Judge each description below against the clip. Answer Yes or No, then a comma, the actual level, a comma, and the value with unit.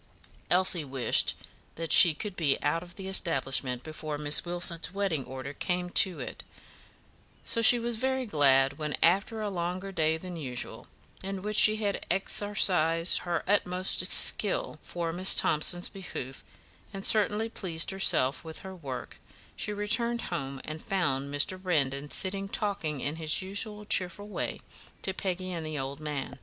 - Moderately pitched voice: Yes, medium, 175 Hz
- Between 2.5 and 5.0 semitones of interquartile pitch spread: Yes, average, 4.5 semitones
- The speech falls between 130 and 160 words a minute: Yes, average, 155 wpm